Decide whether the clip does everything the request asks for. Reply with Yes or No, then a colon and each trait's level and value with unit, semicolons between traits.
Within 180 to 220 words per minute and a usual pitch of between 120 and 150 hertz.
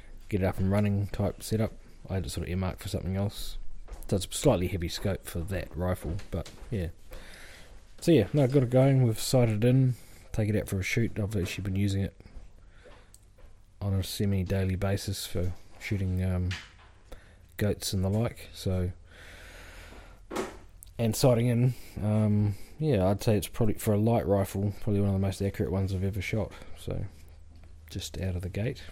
No: average, 185 wpm; very low, 95 Hz